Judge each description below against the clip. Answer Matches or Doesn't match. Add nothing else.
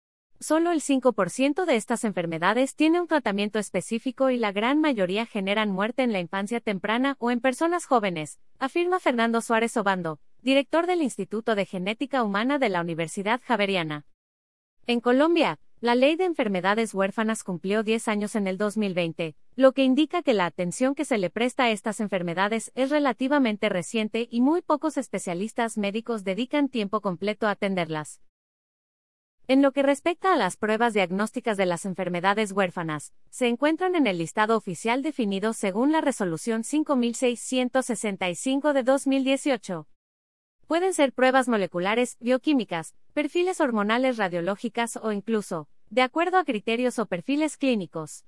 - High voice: Matches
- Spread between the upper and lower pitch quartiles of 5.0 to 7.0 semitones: Matches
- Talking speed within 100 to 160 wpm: Matches